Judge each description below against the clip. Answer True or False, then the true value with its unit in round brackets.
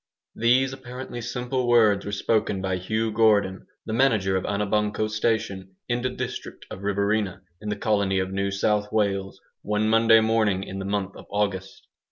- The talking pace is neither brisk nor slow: True (170 wpm)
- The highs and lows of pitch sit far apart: False (2.5 semitones)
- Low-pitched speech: True (105 Hz)